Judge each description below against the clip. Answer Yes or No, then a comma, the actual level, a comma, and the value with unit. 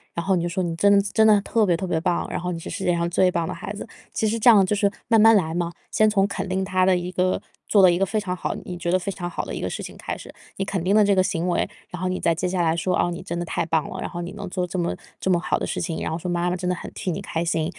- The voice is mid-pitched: Yes, medium, 180 Hz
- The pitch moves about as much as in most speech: No, narrow, 2.2 semitones